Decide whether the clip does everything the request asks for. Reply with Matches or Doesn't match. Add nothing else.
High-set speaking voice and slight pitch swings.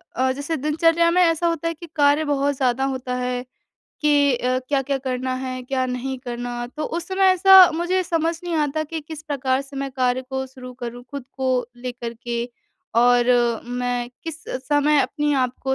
Doesn't match